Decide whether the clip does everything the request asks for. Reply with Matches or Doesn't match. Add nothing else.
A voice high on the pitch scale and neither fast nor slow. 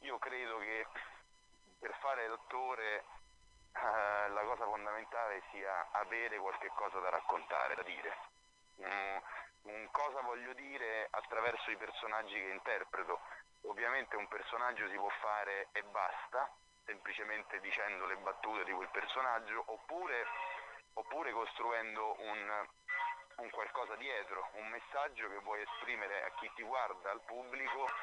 Doesn't match